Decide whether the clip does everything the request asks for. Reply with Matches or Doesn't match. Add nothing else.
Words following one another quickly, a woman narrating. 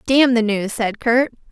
Doesn't match